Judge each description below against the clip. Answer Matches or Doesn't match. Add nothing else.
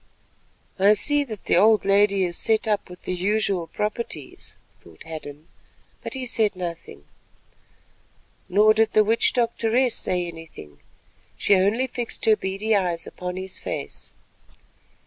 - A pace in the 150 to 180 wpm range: Doesn't match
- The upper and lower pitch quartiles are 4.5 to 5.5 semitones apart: Doesn't match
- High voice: Matches